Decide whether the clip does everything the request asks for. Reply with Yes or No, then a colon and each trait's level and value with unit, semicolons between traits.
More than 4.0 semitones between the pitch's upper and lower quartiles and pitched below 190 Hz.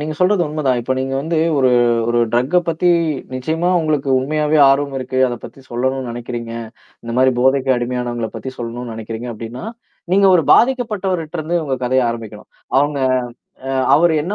Yes: average, 4.5 semitones; low, 135 Hz